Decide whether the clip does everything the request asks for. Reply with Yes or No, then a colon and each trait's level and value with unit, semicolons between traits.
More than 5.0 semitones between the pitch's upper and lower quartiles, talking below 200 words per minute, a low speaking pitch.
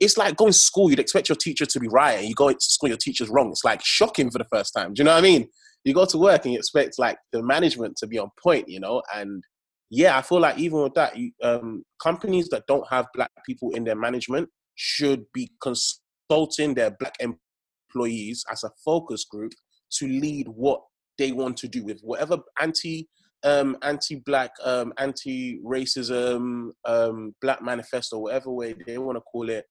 No: wide, 5.4 semitones; fast, 205 wpm; low, 130 Hz